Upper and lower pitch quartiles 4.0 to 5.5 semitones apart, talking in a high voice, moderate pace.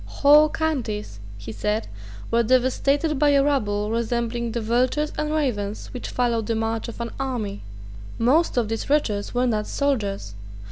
Yes: average, 4.4 semitones; high, 235 Hz; average, 155 wpm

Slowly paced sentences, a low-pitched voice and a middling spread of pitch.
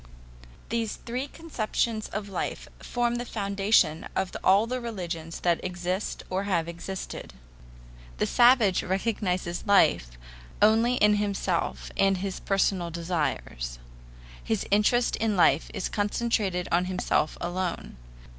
No: slow, 120 wpm; high, 195 Hz; average, 3.8 semitones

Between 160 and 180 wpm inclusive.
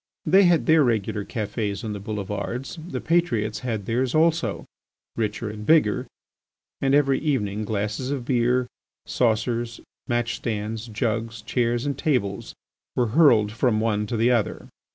No: average, 145 wpm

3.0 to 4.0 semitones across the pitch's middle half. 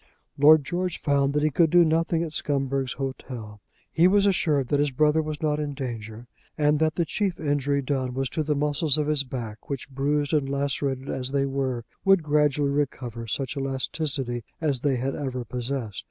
No: narrow, 2.5 semitones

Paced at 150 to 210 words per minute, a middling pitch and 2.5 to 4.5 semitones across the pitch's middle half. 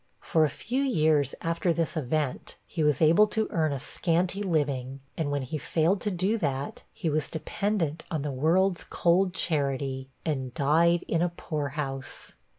Yes: average, 165 wpm; medium, 155 Hz; average, 3.5 semitones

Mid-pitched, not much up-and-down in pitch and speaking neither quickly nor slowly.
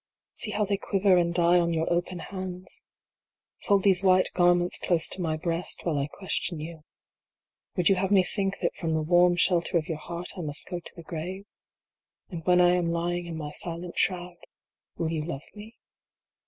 Yes: medium, 175 Hz; narrow, 1.8 semitones; average, 195 wpm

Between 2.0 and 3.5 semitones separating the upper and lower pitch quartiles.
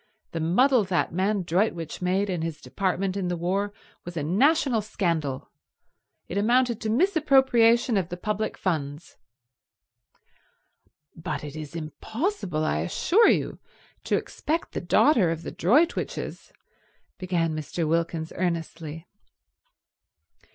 No: wide, 5.5 semitones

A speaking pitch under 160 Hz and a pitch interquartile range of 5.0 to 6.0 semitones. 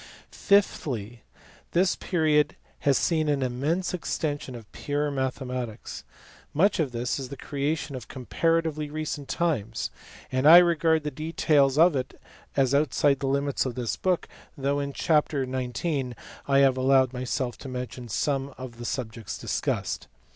No: medium, 140 Hz; average, 3.3 semitones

